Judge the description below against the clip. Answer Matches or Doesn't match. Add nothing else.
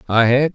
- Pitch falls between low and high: Doesn't match